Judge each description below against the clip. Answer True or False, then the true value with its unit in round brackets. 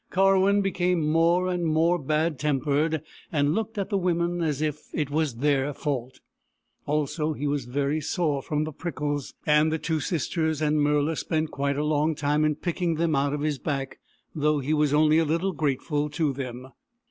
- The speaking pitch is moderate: True (150 Hz)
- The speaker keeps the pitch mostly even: True (2.3 semitones)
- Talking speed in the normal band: True (185 wpm)